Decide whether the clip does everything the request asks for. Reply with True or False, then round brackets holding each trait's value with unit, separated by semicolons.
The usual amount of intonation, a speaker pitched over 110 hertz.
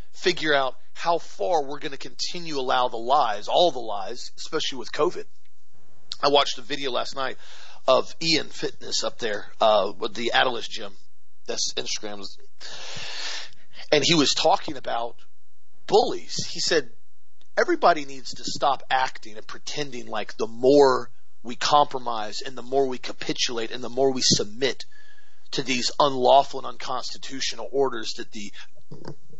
True (3.7 semitones; 140 Hz)